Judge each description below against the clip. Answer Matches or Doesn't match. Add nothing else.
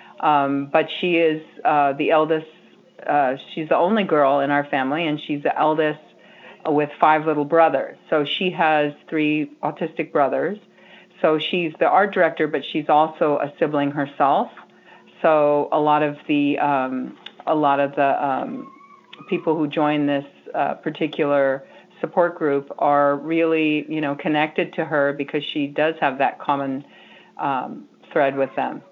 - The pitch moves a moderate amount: Doesn't match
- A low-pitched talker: Doesn't match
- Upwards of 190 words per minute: Doesn't match